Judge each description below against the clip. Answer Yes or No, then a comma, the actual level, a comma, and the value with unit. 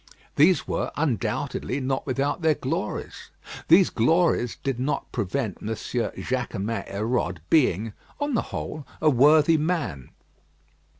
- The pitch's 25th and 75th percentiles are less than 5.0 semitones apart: No, wide, 5.4 semitones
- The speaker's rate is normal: No, slow, 120 wpm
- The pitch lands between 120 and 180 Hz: Yes, low, 135 Hz